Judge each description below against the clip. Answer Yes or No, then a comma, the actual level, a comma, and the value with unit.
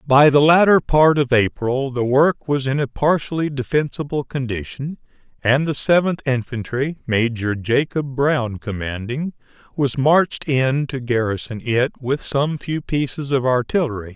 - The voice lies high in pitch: No, low, 135 Hz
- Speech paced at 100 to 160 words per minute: Yes, average, 145 wpm